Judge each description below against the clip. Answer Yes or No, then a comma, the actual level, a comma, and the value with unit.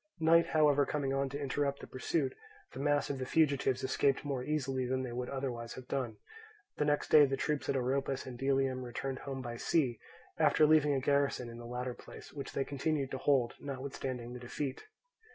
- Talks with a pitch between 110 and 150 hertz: Yes, low, 135 Hz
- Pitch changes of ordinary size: No, narrow, 2.0 semitones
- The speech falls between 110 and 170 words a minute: No, average, 200 wpm